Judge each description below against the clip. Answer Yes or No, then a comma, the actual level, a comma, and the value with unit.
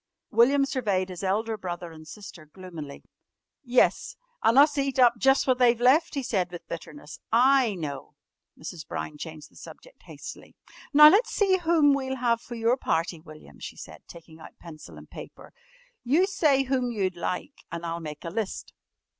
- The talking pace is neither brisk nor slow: Yes, average, 175 wpm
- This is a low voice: No, high, 225 Hz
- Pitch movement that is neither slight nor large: No, wide, 8.0 semitones